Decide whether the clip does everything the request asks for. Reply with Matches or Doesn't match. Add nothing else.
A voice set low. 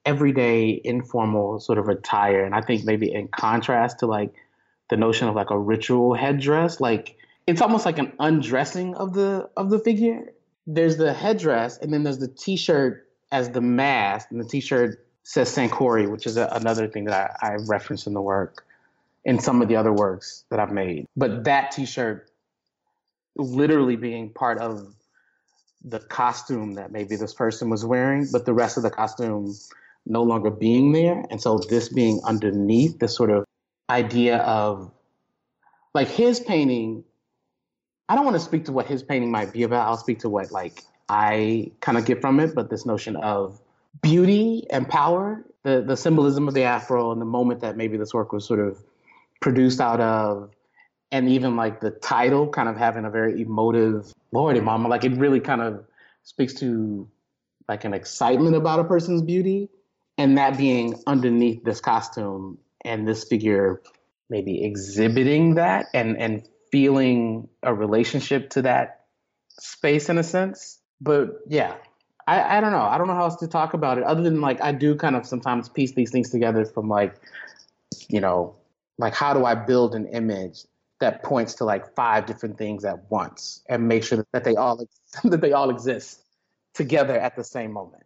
Matches